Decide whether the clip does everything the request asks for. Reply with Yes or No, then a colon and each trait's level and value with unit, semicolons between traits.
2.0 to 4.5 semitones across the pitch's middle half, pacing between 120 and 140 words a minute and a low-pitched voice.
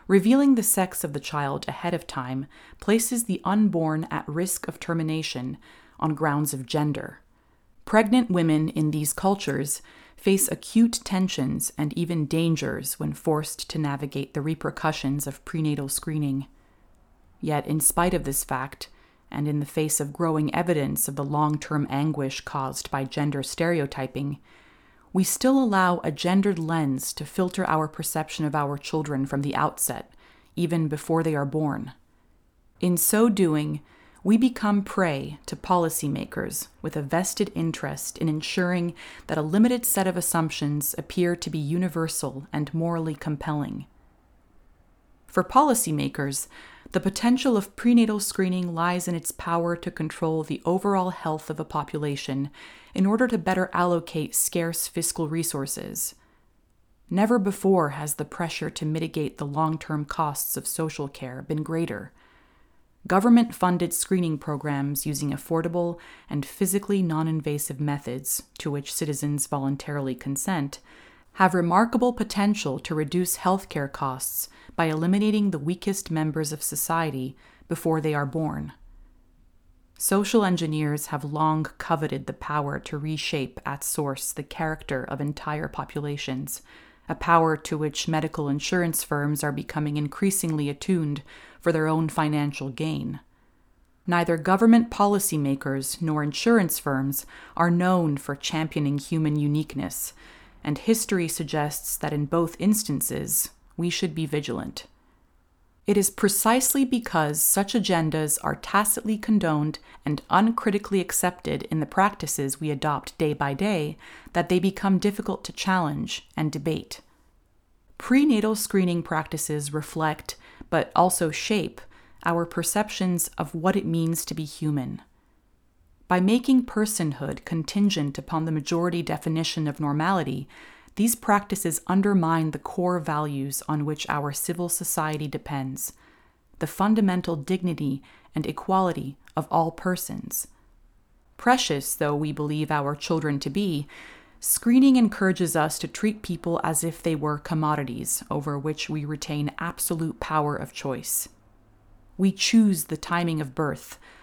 No: average, 4.0 semitones; slow, 135 wpm; medium, 160 Hz